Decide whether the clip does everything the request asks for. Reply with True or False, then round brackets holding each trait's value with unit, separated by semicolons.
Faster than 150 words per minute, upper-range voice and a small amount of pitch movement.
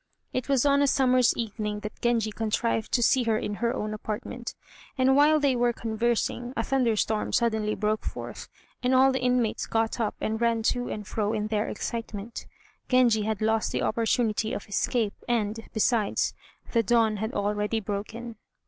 True (175 wpm; 225 Hz; 2.3 semitones)